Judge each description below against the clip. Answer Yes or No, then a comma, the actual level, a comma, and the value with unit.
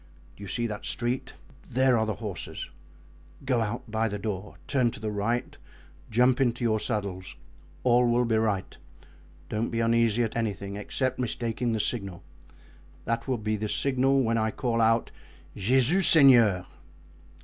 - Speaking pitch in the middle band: No, low, 115 Hz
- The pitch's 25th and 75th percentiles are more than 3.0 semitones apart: No, narrow, 2.5 semitones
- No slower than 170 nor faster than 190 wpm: No, average, 155 wpm